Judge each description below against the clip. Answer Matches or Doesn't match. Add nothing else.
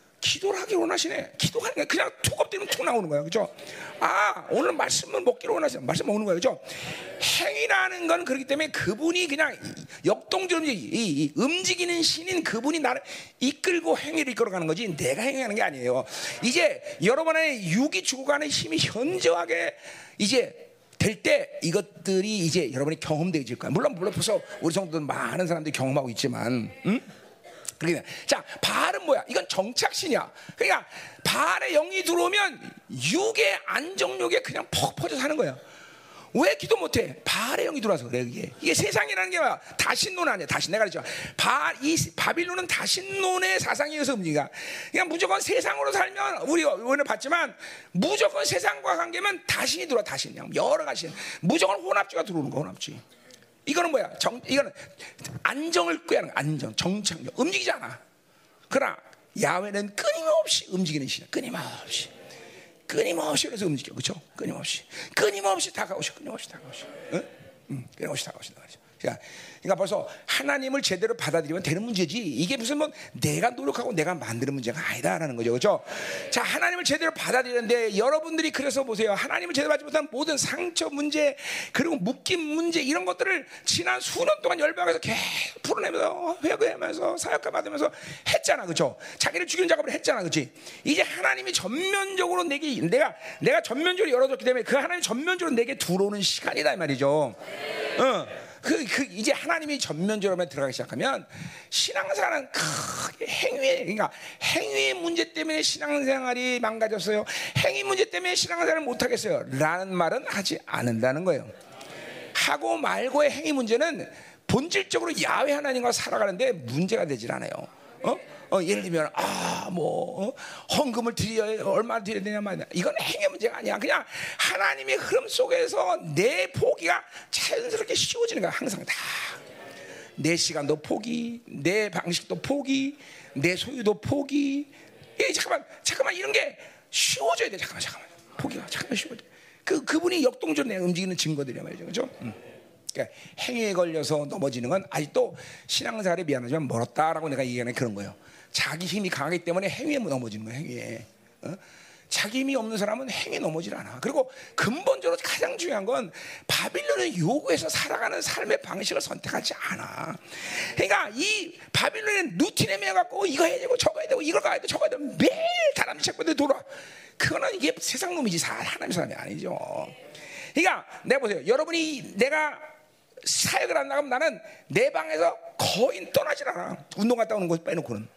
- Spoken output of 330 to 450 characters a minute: Matches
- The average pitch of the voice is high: Matches